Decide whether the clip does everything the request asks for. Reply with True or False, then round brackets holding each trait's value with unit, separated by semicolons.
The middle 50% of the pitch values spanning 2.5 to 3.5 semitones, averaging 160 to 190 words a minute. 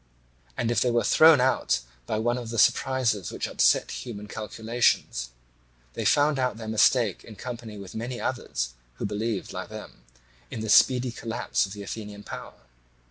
True (2.9 semitones; 170 wpm)